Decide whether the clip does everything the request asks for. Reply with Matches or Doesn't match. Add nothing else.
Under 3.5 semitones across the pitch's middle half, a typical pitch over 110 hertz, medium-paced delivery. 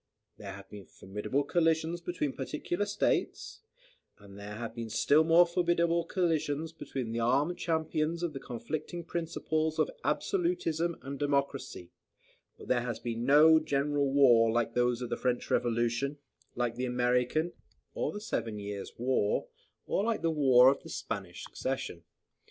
Doesn't match